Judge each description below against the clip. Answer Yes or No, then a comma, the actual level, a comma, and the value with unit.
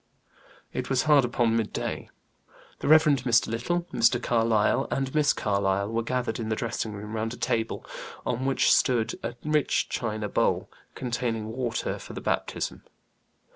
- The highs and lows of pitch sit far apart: No, narrow, 2.6 semitones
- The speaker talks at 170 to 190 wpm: No, average, 155 wpm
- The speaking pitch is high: No, low, 115 Hz